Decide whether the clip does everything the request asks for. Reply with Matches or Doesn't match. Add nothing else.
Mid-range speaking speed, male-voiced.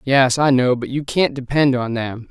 Doesn't match